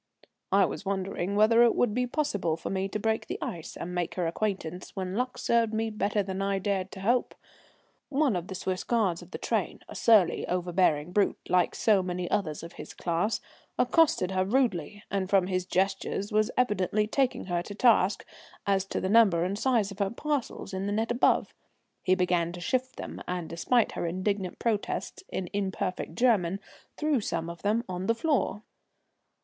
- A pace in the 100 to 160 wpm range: No, average, 190 wpm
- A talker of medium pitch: No, high, 195 Hz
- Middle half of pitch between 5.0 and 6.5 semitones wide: No, average, 3.6 semitones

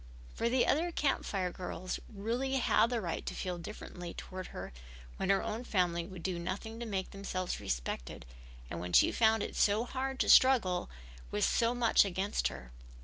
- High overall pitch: Yes, high, 195 Hz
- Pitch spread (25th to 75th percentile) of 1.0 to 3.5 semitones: No, average, 4.7 semitones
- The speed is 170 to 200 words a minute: Yes, average, 185 wpm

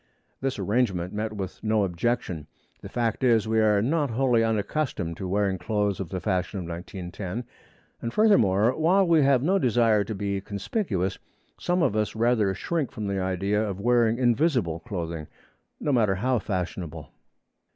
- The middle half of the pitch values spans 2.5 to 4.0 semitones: No, average, 4.5 semitones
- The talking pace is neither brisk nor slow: Yes, average, 160 wpm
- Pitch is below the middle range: Yes, low, 105 Hz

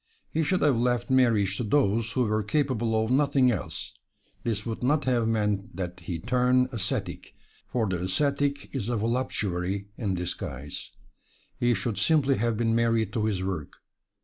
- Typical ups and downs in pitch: Yes, average, 4.2 semitones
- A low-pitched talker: Yes, low, 115 Hz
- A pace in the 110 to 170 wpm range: Yes, average, 165 wpm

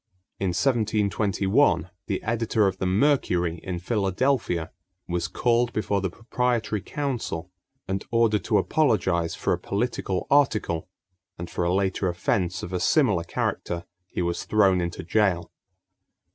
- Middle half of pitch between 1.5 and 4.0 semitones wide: No, average, 4.5 semitones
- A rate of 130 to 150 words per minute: Yes, slow, 135 wpm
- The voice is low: Yes, very low, 95 Hz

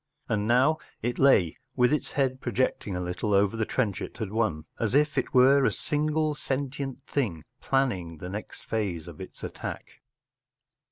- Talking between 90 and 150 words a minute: No, average, 170 wpm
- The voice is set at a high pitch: No, low, 120 Hz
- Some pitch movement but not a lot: No, wide, 6.0 semitones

